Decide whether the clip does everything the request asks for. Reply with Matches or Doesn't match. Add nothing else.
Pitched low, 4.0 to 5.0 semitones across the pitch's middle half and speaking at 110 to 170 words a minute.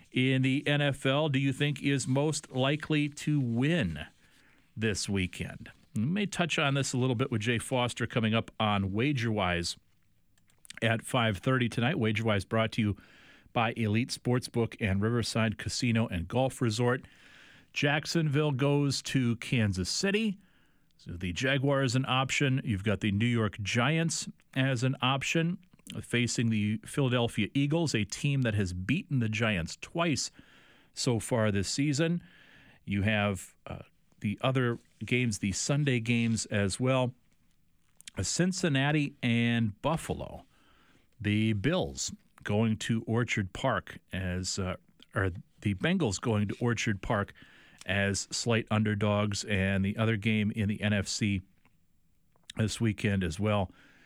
Matches